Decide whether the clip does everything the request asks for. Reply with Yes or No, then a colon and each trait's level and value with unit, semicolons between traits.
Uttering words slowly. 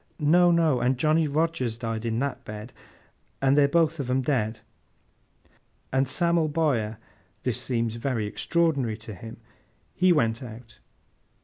Yes: slow, 130 wpm